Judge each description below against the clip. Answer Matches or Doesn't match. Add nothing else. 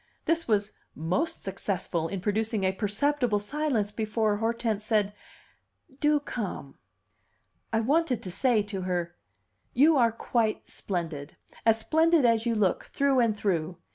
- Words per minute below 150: Matches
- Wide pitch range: Doesn't match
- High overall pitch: Matches